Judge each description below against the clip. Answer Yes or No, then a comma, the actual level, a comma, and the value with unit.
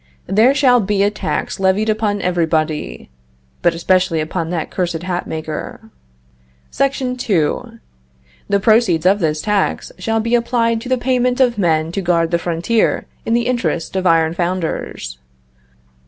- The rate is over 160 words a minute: No, average, 150 wpm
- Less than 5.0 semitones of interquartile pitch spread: No, wide, 5.5 semitones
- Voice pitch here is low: No, high, 190 Hz